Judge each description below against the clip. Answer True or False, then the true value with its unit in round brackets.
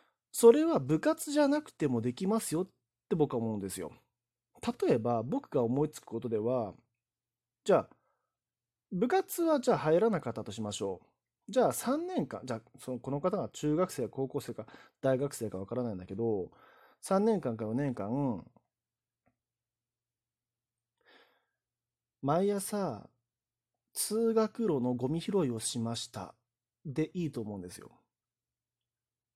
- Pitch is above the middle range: False (125 Hz)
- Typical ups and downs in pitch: False (7.0 semitones)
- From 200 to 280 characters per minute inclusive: True (260 characters per minute)